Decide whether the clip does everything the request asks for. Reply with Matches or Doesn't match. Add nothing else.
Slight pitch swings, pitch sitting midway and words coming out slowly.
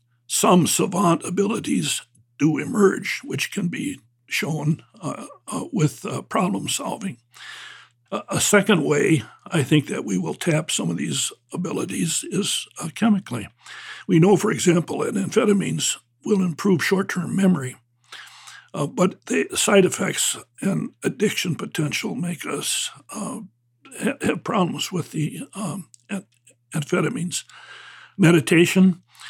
Doesn't match